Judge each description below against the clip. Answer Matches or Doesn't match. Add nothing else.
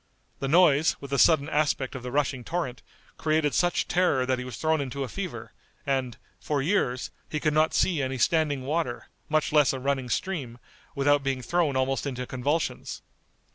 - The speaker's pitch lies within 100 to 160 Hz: Matches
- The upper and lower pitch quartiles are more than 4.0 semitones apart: Doesn't match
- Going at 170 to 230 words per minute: Matches